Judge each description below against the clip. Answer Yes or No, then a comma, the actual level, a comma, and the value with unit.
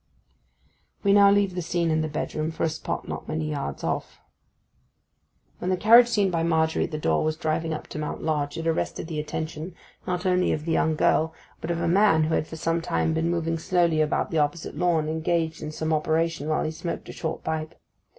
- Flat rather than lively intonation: Yes, narrow, 1.6 semitones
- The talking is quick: Yes, fast, 220 wpm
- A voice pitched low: No, medium, 160 Hz